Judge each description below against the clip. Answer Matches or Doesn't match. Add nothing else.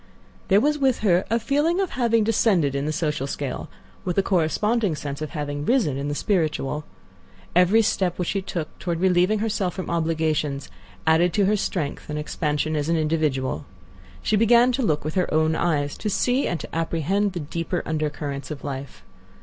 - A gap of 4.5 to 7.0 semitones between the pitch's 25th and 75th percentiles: Matches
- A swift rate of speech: Doesn't match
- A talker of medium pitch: Matches